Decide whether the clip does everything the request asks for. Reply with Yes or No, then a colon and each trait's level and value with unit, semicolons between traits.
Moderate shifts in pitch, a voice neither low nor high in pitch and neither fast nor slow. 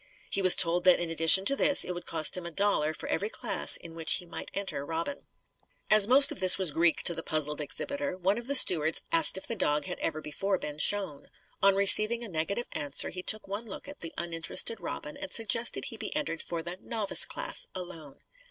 No: average, 4.6 semitones; medium, 180 Hz; fast, 225 wpm